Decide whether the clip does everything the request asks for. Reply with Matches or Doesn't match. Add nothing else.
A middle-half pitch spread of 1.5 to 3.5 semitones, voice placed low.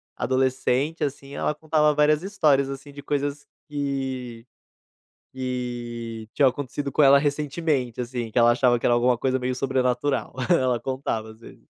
Matches